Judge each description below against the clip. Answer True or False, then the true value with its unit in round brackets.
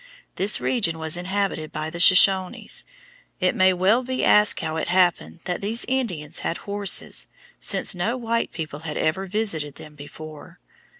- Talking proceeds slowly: False (160 wpm)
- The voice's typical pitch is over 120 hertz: True (185 Hz)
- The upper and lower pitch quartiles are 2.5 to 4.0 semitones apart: False (4.4 semitones)